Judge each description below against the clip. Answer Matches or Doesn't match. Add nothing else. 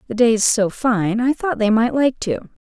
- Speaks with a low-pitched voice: Doesn't match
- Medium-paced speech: Doesn't match